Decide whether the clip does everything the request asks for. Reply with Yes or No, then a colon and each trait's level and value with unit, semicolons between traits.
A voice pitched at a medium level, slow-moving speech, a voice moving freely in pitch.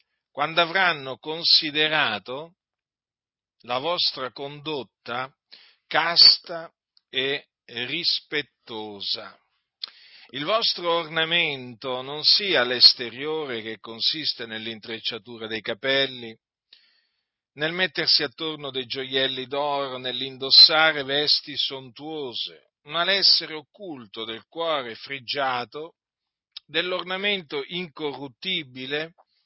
No: medium, 145 Hz; slow, 75 wpm; average, 4.2 semitones